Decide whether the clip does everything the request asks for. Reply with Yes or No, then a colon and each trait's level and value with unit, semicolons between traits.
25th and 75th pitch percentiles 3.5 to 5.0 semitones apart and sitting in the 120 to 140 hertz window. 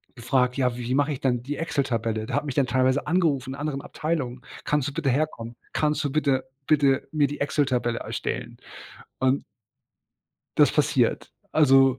No: narrow, 2.6 semitones; low, 135 Hz